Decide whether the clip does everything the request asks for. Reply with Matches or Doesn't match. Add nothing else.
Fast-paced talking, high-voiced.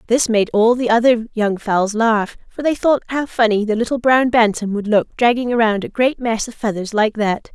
Matches